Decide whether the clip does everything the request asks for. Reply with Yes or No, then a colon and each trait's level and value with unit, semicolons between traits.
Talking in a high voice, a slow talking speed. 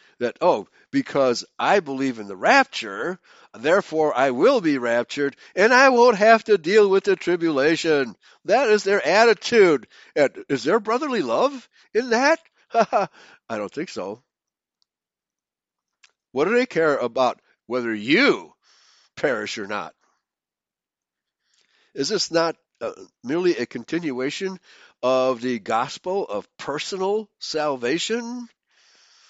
Yes: high, 195 Hz; slow, 125 wpm